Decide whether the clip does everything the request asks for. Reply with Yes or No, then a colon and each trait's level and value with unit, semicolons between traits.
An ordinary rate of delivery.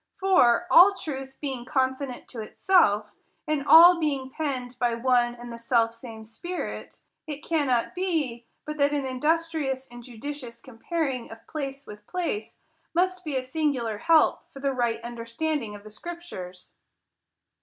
Yes: average, 150 wpm